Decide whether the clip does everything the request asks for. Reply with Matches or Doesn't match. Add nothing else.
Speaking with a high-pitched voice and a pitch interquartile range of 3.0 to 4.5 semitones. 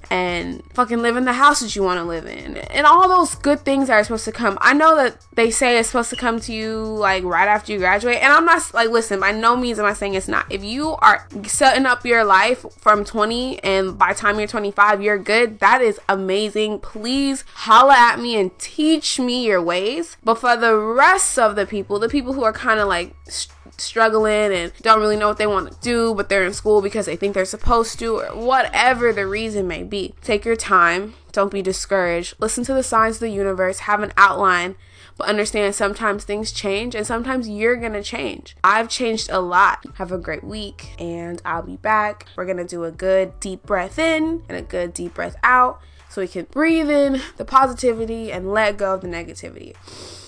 Matches